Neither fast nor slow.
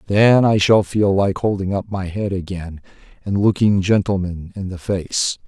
Yes: average, 175 wpm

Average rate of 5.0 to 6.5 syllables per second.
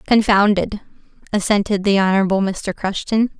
Yes: 5.3 syllables/s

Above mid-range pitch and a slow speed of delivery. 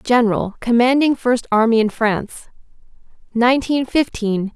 Yes: high, 235 Hz; slow, 105 wpm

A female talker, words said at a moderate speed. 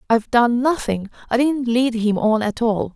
No: female; fast, 225 wpm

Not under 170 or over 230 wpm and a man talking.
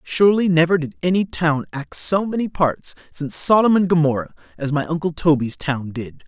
Yes: average, 180 wpm; male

